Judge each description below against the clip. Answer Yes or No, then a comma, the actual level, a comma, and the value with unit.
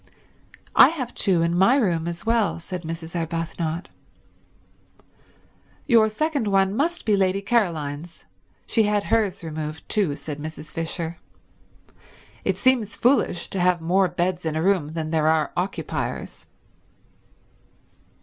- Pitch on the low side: No, medium, 180 Hz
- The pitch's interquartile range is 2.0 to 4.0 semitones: No, average, 4.5 semitones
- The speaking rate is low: Yes, slow, 130 wpm